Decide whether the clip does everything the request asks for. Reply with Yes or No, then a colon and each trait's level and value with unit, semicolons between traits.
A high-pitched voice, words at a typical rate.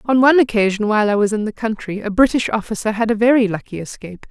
No: high, 220 Hz; fast, 235 wpm